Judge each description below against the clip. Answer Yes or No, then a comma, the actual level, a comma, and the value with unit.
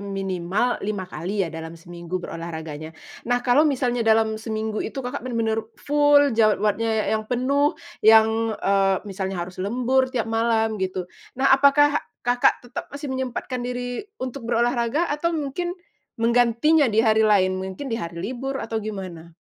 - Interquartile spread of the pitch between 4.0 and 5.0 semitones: Yes, average, 4.6 semitones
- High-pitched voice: Yes, high, 225 Hz